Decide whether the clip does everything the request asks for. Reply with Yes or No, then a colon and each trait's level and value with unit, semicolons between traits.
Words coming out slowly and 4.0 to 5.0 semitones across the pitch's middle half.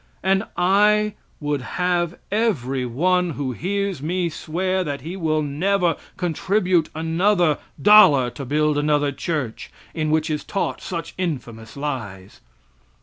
Yes: slow, 130 wpm; average, 4.3 semitones